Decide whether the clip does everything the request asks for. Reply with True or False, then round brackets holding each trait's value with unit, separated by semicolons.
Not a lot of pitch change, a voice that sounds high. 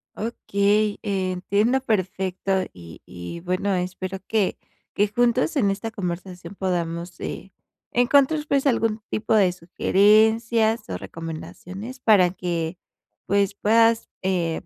False (3.7 semitones; 200 Hz)